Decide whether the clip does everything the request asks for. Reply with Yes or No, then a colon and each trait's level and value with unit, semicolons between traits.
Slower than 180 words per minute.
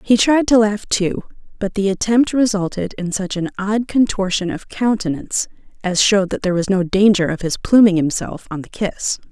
No: average, 195 wpm